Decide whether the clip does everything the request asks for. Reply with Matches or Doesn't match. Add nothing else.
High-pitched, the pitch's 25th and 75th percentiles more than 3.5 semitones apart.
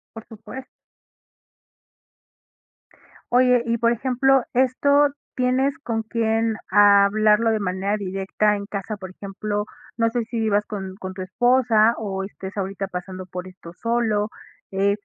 Doesn't match